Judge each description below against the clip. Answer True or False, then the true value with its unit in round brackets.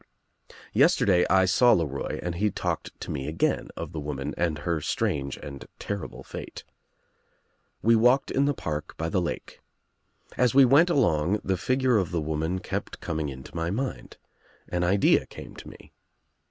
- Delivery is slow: False (180 wpm)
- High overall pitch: False (90 Hz)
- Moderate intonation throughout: False (6.7 semitones)